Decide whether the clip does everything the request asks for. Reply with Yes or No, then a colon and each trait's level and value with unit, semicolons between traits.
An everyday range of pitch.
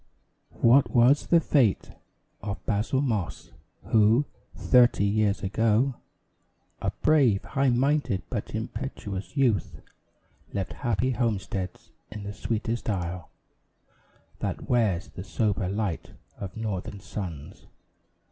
Yes: average, 3.9 semitones